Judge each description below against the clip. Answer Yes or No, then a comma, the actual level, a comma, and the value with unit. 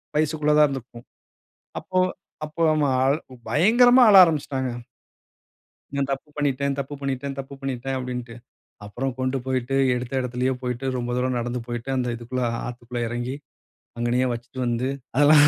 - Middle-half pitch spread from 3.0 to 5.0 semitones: No, narrow, 2.4 semitones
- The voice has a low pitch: Yes, low, 130 Hz